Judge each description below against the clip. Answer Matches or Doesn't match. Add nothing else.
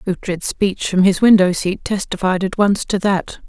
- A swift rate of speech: Doesn't match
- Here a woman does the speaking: Matches